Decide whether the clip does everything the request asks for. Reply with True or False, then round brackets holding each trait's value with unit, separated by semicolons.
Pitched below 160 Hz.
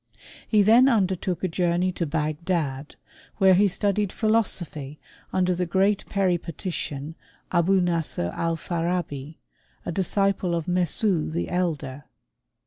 False (175 Hz)